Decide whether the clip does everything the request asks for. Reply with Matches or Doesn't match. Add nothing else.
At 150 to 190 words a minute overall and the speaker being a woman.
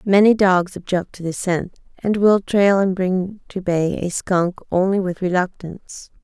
Matches